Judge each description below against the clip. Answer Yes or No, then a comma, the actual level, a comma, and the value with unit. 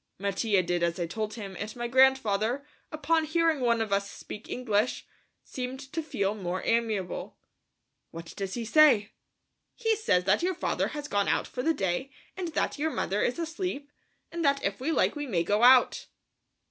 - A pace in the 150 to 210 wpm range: Yes, average, 185 wpm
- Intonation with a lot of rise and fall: Yes, wide, 6.6 semitones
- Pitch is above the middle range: Yes, high, 235 Hz